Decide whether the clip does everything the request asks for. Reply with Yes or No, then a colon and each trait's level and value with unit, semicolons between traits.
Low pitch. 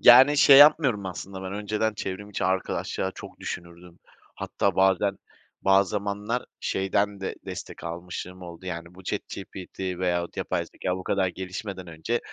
Yes: very low, 95 Hz